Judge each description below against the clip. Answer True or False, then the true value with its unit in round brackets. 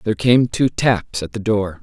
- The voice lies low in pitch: True (110 Hz)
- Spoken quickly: True (230 wpm)